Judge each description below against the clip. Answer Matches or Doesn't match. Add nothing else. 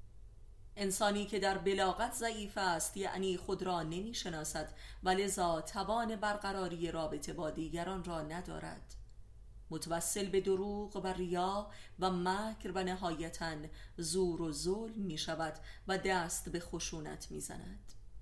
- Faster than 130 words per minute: Doesn't match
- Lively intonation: Doesn't match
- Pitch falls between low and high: Matches